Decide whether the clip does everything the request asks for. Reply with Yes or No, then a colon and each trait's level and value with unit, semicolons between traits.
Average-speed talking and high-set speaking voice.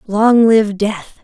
Yes: average, 145 wpm; high, 210 Hz